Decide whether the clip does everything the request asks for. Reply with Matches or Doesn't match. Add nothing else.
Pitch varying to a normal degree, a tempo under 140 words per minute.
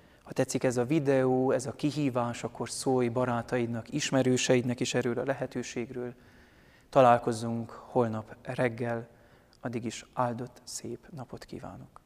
Doesn't match